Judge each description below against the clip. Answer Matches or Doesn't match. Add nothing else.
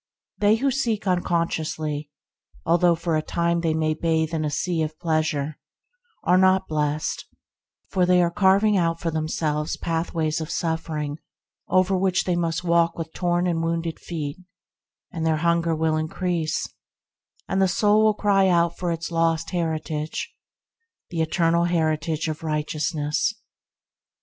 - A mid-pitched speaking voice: Matches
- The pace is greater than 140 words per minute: Matches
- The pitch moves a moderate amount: Doesn't match